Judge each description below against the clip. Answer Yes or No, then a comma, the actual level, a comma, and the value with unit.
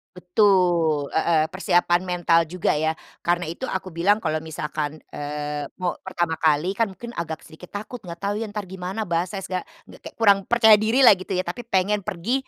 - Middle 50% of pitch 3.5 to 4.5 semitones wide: Yes, average, 3.9 semitones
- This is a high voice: No, medium, 180 Hz